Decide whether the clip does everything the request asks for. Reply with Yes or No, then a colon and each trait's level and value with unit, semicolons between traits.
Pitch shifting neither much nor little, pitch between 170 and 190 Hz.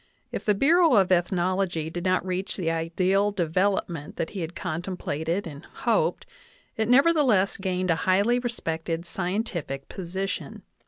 Yes: average, 3.2 semitones; medium, 185 Hz